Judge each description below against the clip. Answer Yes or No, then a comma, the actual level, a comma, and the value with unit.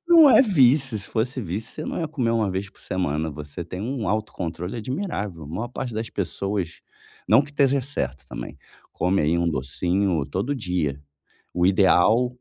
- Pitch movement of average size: No, wide, 6.8 semitones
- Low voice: Yes, low, 100 Hz